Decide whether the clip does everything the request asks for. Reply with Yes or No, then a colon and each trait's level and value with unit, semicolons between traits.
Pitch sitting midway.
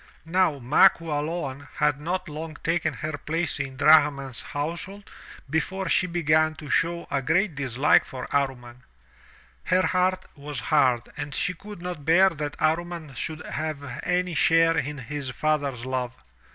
Yes: medium, 155 Hz